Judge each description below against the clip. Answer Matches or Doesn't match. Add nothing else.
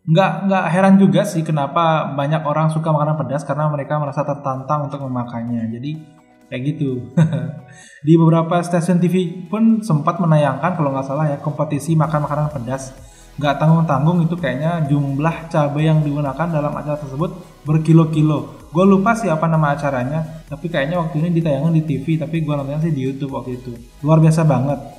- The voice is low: Doesn't match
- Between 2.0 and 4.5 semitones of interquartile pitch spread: Matches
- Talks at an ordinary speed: Doesn't match